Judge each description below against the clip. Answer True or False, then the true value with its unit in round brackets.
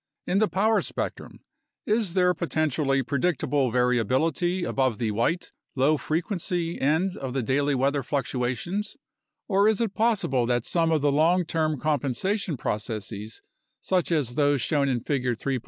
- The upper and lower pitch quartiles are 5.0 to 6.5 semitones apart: True (5.6 semitones)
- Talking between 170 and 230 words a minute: False (150 wpm)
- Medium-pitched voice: True (150 Hz)